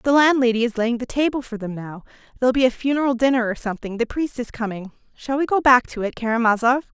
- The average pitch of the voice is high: Yes, high, 240 Hz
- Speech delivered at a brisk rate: Yes, fast, 225 wpm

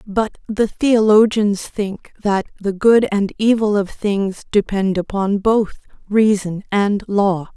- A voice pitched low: No, high, 205 Hz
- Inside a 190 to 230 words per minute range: No, slow, 135 wpm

